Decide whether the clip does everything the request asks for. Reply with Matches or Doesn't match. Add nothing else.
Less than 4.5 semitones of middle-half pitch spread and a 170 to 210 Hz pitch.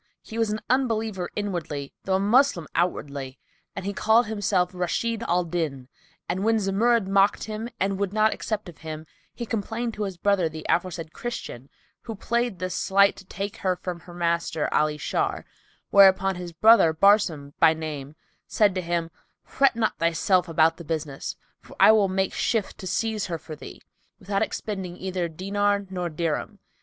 Matches